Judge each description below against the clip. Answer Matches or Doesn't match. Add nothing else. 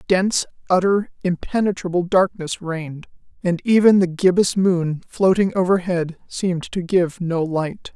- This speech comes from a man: Doesn't match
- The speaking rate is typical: Doesn't match